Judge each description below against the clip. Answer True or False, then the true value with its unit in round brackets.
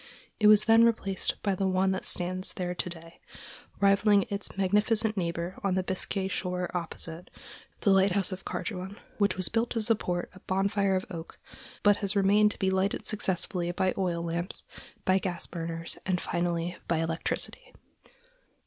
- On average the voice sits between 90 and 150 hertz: False (190 Hz)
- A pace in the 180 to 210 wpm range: False (165 wpm)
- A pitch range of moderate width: False (2.2 semitones)